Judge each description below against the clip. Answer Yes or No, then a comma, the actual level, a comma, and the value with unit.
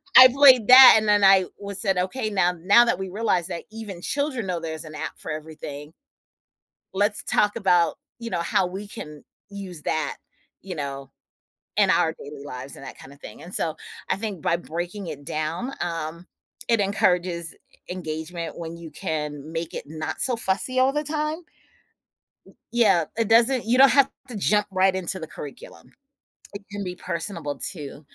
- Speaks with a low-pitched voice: No, medium, 185 Hz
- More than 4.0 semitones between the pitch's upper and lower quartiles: Yes, average, 5.1 semitones